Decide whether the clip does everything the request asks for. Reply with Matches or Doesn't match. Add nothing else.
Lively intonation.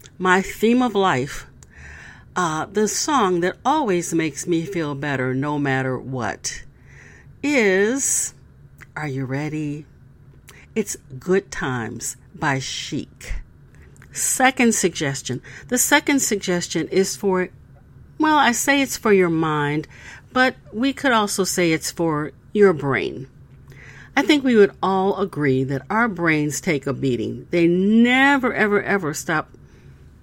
Matches